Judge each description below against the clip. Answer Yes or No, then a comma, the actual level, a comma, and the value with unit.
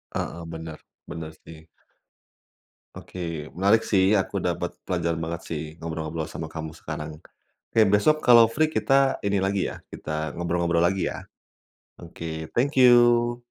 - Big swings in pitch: Yes, wide, 6.5 semitones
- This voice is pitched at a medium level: No, very low, 85 Hz